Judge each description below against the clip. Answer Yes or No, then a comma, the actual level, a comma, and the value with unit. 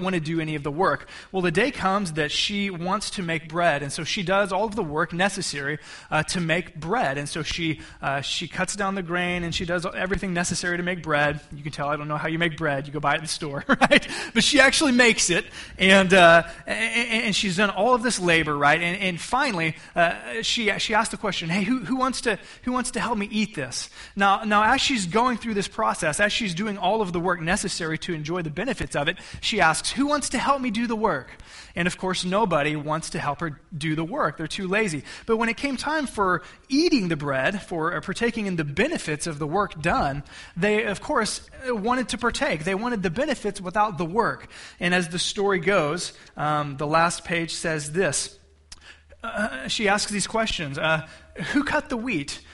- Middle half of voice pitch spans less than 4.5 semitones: No, average, 5.3 semitones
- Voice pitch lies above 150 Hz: Yes, medium, 185 Hz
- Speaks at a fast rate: Yes, fast, 230 wpm